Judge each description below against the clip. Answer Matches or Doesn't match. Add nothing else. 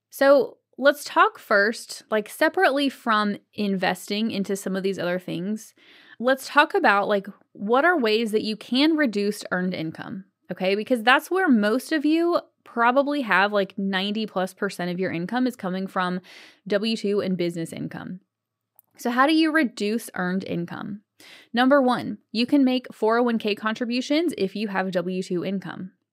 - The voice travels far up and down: Matches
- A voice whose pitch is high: Matches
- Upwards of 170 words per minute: Doesn't match